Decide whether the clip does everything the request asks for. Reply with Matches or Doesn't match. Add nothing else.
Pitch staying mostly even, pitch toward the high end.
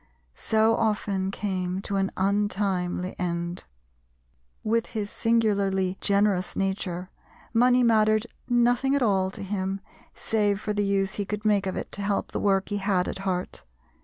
Matches